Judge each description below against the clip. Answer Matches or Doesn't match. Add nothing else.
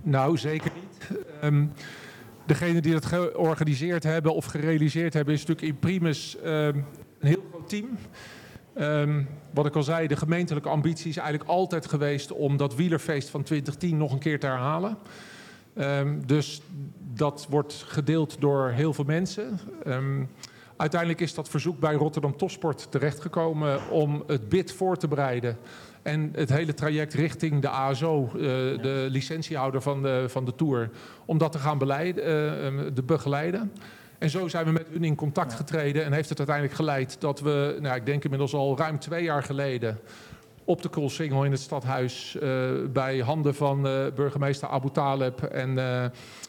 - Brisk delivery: Doesn't match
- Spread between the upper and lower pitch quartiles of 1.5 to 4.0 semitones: Matches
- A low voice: Doesn't match